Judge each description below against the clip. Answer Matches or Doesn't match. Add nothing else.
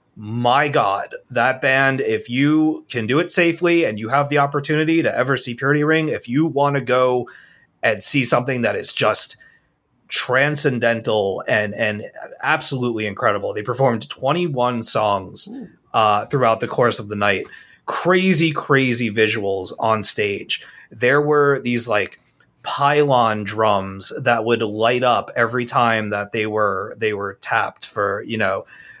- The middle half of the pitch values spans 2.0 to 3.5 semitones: Doesn't match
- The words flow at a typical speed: Matches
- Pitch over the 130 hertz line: Doesn't match